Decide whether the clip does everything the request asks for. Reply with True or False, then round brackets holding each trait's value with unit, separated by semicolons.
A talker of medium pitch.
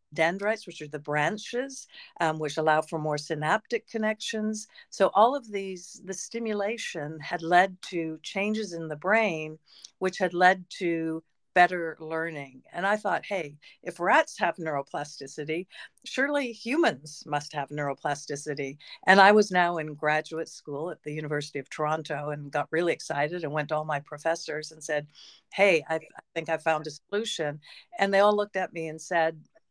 True (165 Hz)